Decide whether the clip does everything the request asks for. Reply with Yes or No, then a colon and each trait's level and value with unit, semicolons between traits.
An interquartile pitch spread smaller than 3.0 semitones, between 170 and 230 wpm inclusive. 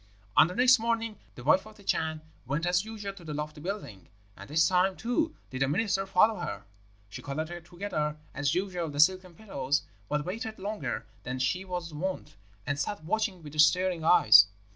No: average, 5.0 semitones; average, 185 wpm